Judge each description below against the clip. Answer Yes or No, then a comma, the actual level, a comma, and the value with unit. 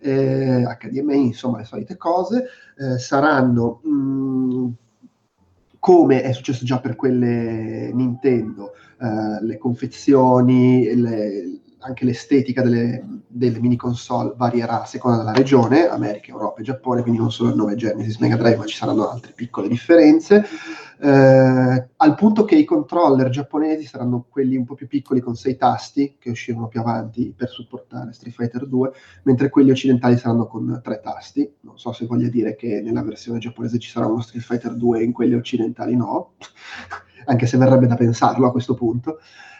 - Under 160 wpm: No, average, 165 wpm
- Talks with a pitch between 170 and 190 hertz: No, low, 125 Hz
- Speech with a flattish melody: Yes, narrow, 2.3 semitones